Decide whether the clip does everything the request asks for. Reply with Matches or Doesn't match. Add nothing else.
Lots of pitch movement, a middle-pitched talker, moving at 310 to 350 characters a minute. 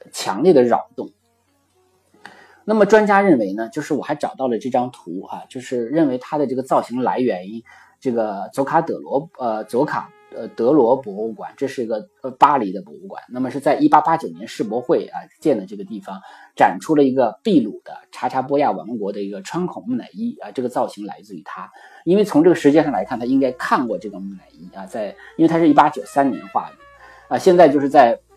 Matches